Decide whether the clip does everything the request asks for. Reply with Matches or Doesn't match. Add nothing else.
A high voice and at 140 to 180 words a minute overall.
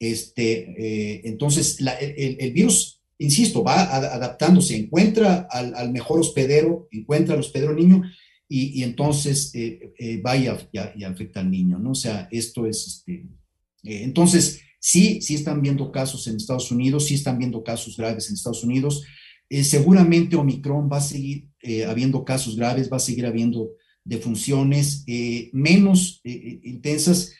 Doesn't match